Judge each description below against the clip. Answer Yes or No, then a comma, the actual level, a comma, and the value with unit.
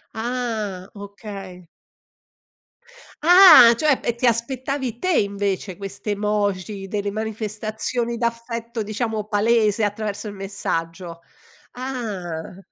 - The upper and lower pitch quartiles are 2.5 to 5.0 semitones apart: Yes, average, 2.8 semitones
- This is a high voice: Yes, high, 215 Hz